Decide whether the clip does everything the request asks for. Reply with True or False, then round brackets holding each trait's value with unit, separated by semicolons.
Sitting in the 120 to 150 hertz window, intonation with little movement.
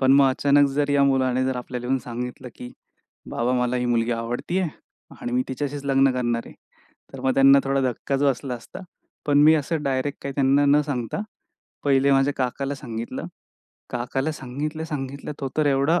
True (135 Hz; 2.3 semitones)